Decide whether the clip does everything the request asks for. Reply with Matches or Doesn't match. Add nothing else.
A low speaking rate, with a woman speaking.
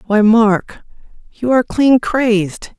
Matches